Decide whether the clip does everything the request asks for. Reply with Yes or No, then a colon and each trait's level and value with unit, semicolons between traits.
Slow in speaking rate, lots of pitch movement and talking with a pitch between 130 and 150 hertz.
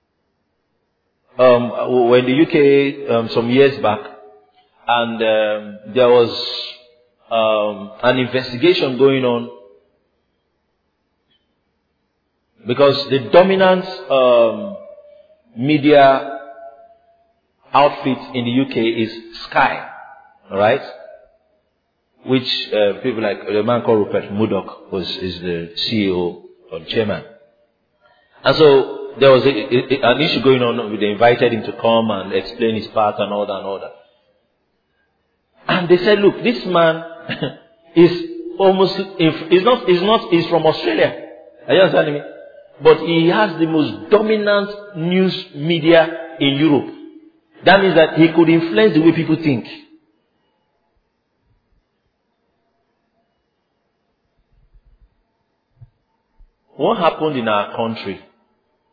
Yes: slow, 120 wpm; wide, 7.8 semitones; medium, 140 Hz